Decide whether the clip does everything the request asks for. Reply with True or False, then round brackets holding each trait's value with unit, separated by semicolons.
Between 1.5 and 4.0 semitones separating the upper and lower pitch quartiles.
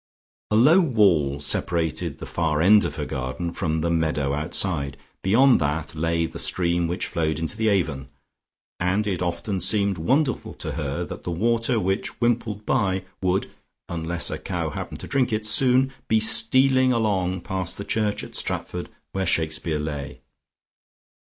False (5.2 semitones)